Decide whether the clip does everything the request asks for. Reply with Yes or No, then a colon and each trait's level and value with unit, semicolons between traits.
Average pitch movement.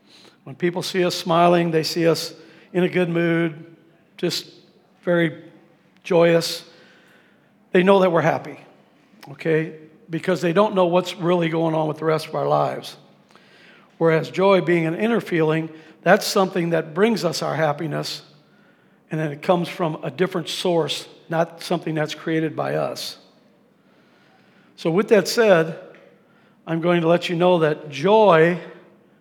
No: narrow, 2.2 semitones